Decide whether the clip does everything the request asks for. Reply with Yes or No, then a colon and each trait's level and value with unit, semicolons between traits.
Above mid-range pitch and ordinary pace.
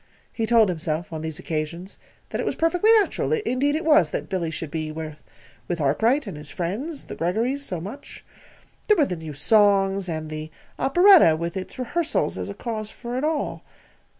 Yes: high, 195 Hz; average, 185 wpm